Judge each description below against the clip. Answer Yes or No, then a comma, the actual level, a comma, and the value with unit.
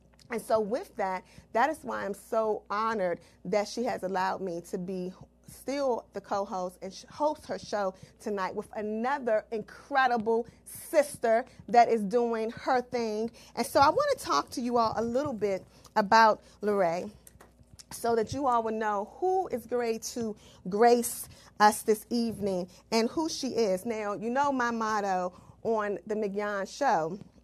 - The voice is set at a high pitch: Yes, high, 225 Hz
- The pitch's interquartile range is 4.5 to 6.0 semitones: No, average, 3.0 semitones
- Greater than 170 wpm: No, average, 165 wpm